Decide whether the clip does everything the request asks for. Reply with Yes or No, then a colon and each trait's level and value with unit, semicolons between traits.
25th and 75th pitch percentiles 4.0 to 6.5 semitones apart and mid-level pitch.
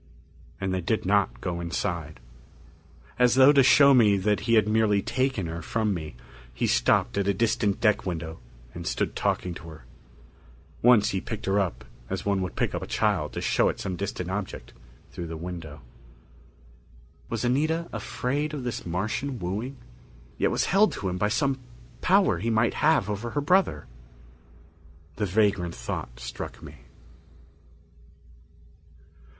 No: wide, 5.5 semitones; low, 100 Hz